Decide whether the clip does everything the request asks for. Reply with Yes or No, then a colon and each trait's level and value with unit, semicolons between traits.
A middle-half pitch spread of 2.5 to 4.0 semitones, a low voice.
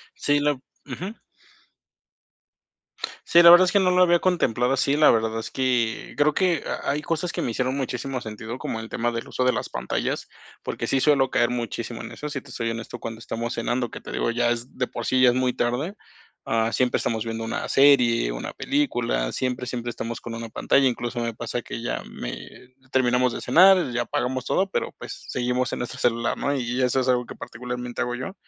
Yes: average, 2.9 semitones; low, 125 Hz